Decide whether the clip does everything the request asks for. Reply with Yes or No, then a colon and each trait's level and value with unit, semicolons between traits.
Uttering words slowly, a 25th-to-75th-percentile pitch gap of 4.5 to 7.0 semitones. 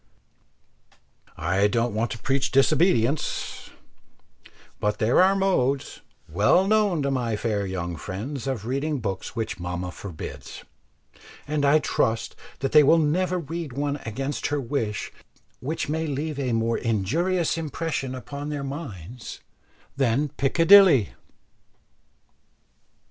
Yes: slow, 120 wpm; wide, 5.5 semitones